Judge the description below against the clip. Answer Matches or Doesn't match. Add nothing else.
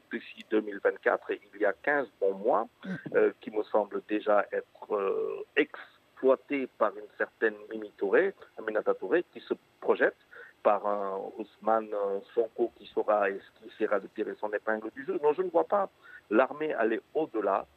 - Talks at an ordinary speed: Matches